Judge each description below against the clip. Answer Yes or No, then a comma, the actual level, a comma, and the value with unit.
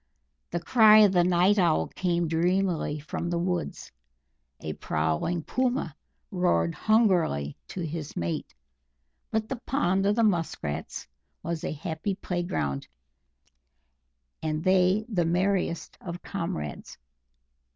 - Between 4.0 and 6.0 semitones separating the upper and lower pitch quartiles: No, average, 3.6 semitones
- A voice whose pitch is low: No, medium, 175 Hz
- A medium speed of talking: No, slow, 120 wpm